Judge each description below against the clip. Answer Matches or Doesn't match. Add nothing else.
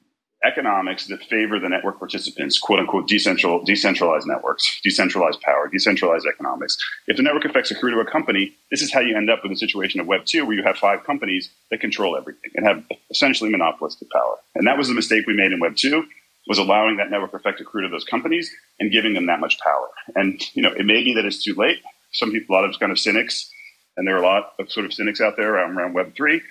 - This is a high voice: Matches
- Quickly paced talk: Matches